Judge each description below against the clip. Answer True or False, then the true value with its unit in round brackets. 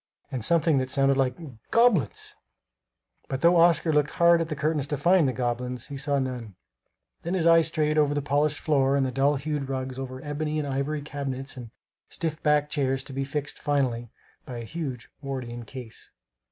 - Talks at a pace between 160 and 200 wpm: True (190 wpm)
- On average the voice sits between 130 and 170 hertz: True (140 Hz)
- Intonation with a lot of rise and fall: False (2.7 semitones)